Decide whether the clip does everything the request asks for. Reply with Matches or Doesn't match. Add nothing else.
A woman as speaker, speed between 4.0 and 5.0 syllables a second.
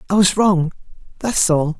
Doesn't match